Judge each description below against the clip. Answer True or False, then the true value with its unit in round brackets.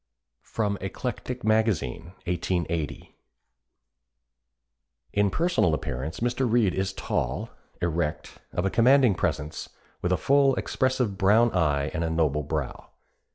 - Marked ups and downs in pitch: True (6.7 semitones)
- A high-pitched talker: False (95 Hz)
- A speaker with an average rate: False (115 wpm)